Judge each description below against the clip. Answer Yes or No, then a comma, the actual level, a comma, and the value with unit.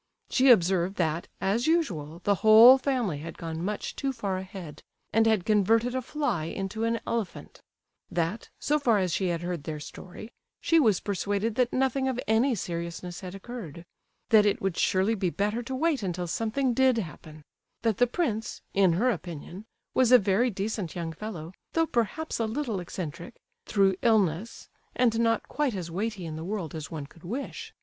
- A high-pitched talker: Yes, high, 205 Hz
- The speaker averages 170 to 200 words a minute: Yes, average, 180 wpm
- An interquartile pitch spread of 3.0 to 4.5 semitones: No, average, 5.2 semitones